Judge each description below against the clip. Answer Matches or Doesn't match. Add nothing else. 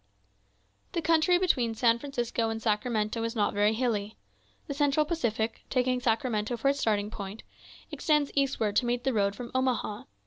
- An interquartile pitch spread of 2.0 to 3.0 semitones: Doesn't match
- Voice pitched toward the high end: Matches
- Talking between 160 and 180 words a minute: Matches